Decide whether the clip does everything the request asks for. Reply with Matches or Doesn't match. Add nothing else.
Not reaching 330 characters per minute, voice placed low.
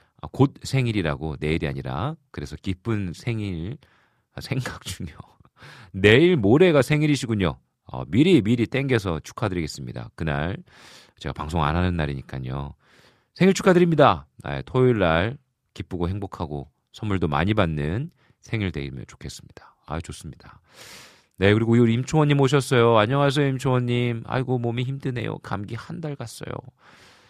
Matches